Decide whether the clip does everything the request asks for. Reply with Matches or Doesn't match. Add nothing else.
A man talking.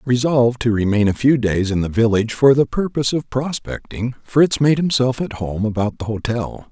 Matches